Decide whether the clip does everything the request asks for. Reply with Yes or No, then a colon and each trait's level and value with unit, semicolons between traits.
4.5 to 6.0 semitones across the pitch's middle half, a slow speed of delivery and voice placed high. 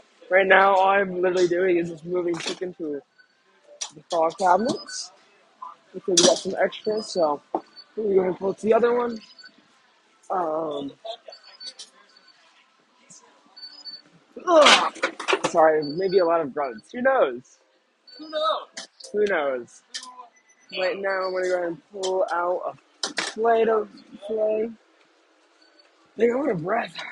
Yes: average, 5.2 semitones; slow, 130 wpm; high, 195 Hz